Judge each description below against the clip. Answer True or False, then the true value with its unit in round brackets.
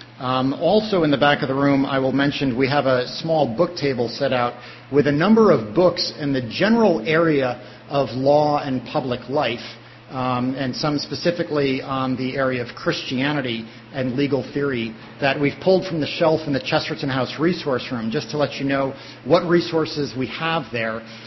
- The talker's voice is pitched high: False (140 Hz)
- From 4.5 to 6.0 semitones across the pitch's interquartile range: False (3.2 semitones)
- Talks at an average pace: True (190 wpm)